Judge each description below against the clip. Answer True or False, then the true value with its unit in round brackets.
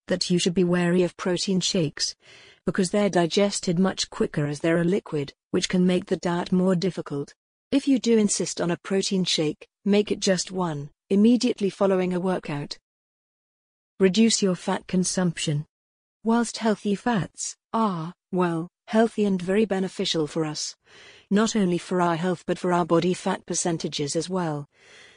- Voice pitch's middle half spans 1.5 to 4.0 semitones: True (2.6 semitones)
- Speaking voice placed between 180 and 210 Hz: True (185 Hz)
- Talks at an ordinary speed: True (160 wpm)